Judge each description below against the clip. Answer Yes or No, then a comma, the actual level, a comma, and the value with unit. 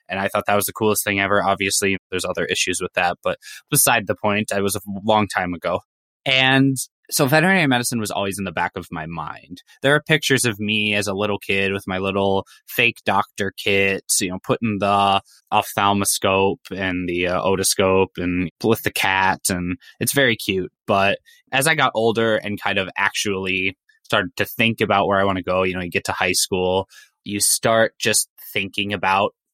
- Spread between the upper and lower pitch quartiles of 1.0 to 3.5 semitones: Yes, narrow, 2.5 semitones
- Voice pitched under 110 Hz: Yes, low, 100 Hz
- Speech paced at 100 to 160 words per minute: No, average, 200 wpm